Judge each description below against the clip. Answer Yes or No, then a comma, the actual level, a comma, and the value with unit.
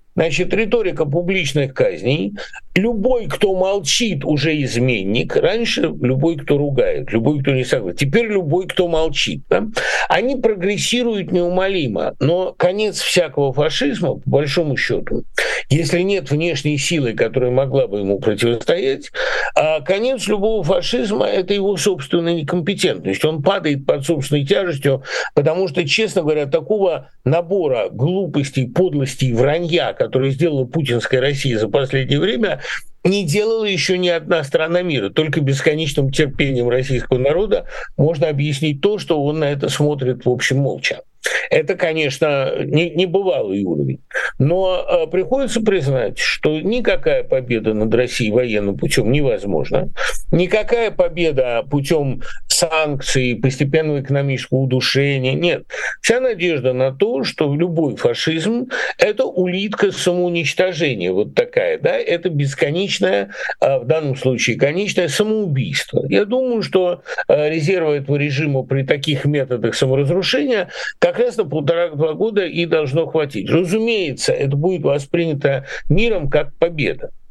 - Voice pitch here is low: No, medium, 160 Hz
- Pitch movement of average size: No, wide, 5.7 semitones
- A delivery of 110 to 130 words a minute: Yes, average, 125 wpm